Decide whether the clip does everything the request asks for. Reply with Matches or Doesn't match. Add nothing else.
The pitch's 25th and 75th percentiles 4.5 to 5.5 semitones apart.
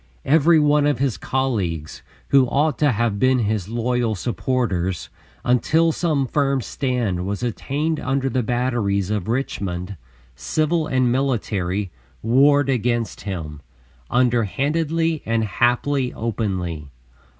Matches